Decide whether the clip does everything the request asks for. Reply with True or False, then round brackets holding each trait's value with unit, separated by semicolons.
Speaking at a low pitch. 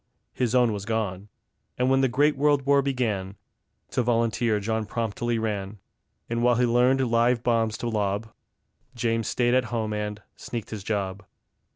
True (115 Hz)